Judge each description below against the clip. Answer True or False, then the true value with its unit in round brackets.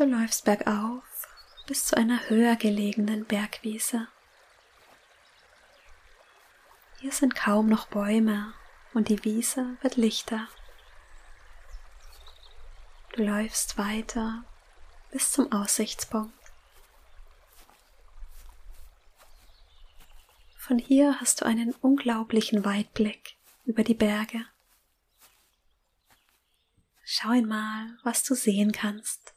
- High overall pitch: True (220 Hz)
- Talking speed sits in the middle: False (85 wpm)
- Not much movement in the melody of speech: True (2.2 semitones)